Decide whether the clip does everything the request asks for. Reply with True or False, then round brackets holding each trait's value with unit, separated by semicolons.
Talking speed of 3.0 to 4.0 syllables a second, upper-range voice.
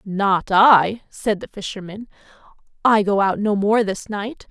True (3.9 syllables/s; 205 Hz)